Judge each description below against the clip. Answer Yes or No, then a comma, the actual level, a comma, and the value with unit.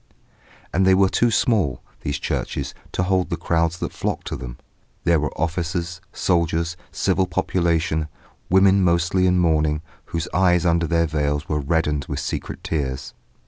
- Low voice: Yes, very low, 85 Hz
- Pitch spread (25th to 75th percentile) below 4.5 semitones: Yes, average, 2.8 semitones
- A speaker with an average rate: Yes, average, 155 wpm